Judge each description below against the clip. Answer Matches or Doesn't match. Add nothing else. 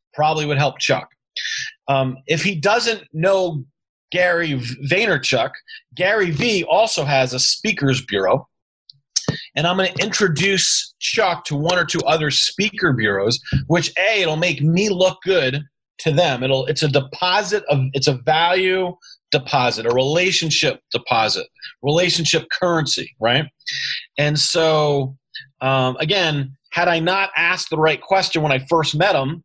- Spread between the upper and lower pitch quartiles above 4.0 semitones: Matches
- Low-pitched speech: Doesn't match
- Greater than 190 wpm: Doesn't match